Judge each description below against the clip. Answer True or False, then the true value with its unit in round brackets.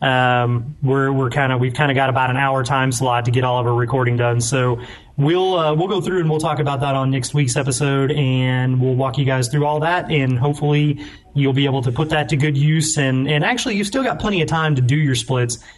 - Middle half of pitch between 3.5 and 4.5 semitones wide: False (2.7 semitones)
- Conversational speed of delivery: False (260 wpm)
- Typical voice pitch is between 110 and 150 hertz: True (135 Hz)